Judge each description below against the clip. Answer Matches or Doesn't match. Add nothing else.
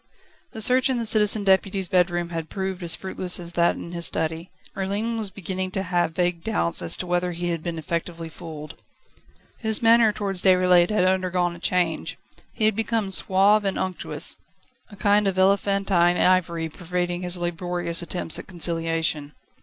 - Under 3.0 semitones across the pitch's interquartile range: Matches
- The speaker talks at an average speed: Matches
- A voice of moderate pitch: Matches